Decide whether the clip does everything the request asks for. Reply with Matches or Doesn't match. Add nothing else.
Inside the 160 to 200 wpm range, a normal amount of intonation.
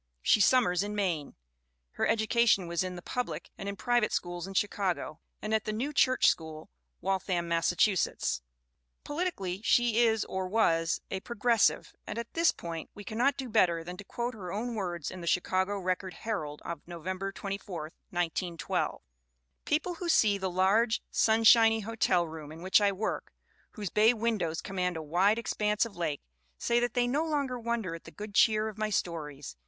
Matches